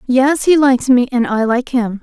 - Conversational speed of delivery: No, fast, 235 wpm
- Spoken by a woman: Yes, female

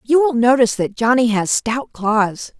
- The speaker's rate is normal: Yes, average, 185 wpm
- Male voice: No, female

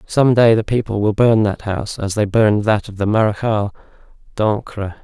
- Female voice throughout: No, male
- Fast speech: No, average, 190 wpm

